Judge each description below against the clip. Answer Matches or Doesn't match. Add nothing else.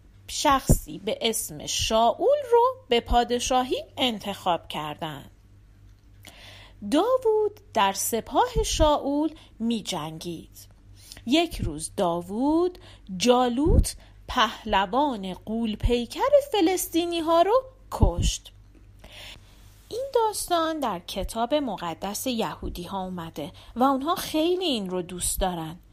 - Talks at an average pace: Doesn't match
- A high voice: Matches